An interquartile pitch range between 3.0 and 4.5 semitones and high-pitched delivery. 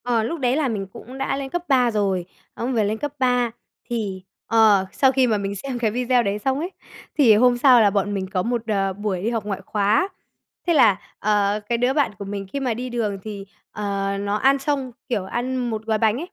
Yes: average, 3.9 semitones; high, 225 Hz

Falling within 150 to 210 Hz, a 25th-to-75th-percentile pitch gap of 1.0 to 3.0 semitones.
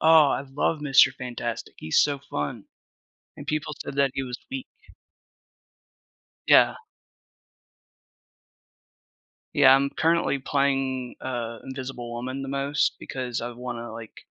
No: low, 135 Hz; narrow, 2.5 semitones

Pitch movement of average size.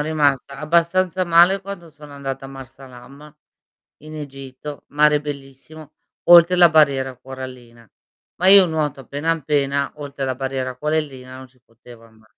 Yes: average, 3.1 semitones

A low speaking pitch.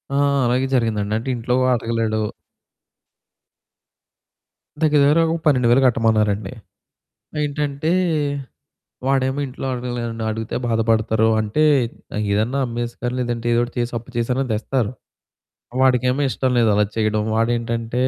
Yes: low, 120 Hz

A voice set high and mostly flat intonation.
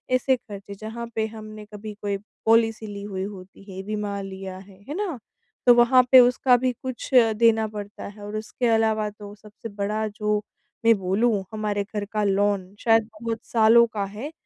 Yes: high, 215 Hz; narrow, 2.1 semitones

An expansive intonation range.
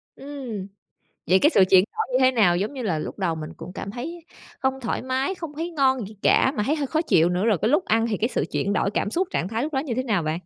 Yes: wide, 6.4 semitones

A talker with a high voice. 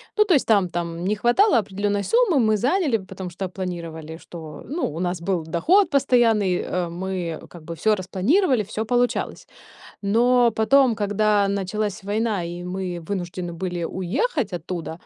Yes: high, 195 Hz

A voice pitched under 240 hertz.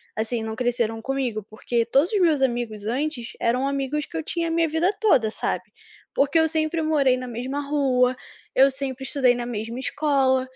No: very high, 265 Hz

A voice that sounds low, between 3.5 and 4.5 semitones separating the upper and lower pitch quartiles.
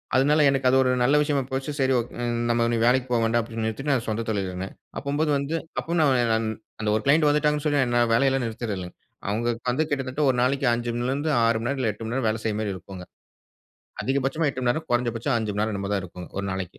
Yes: low, 120 Hz; average, 3.8 semitones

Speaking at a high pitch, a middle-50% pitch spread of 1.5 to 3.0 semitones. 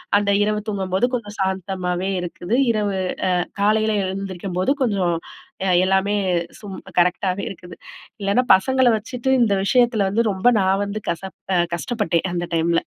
Yes: high, 195 Hz; narrow, 2.5 semitones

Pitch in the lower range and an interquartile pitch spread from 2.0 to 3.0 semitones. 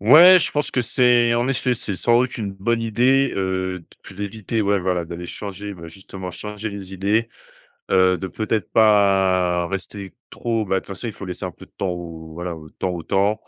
No: low, 100 Hz; average, 3.6 semitones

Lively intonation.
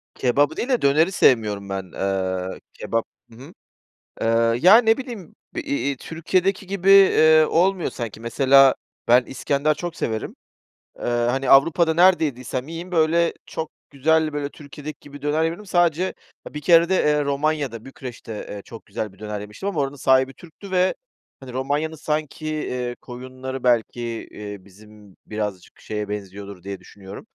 Yes: wide, 6.1 semitones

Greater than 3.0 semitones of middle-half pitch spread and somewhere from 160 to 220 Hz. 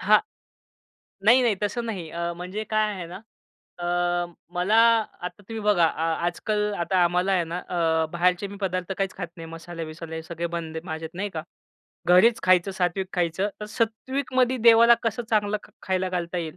Yes: average, 3.6 semitones; medium, 185 Hz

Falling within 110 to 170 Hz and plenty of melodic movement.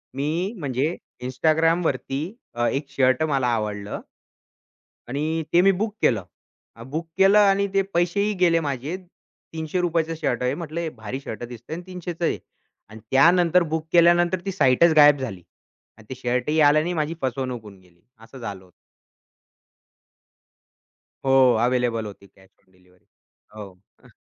Yes: medium, 140 Hz; wide, 6.3 semitones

